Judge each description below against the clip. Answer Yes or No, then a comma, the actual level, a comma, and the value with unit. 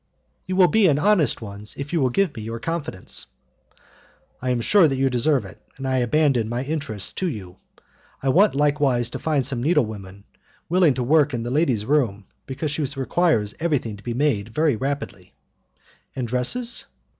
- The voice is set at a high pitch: No, low, 135 Hz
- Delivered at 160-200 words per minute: Yes, average, 180 wpm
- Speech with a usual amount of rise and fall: Yes, average, 5.0 semitones